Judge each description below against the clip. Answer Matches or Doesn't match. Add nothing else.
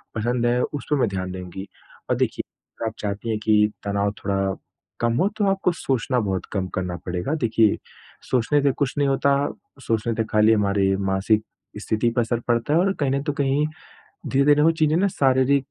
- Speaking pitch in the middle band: Doesn't match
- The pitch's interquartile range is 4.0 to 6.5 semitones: Matches